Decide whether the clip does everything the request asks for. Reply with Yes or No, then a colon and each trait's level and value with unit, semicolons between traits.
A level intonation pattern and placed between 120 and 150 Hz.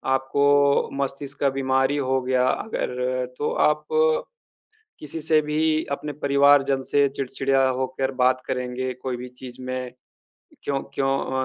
Yes: narrow, 1.7 semitones; low, 135 Hz